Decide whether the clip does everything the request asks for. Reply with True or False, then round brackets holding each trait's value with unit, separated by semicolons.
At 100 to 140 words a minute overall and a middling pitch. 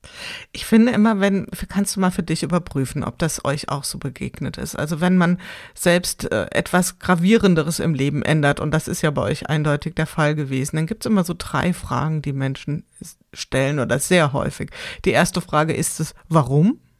False (190 wpm; 160 Hz)